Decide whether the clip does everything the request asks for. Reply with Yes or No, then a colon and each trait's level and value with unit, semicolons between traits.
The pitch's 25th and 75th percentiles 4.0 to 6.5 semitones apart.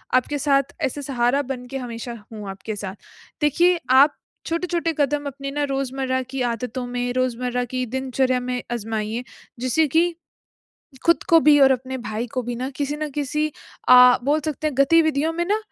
No: average, 3.1 semitones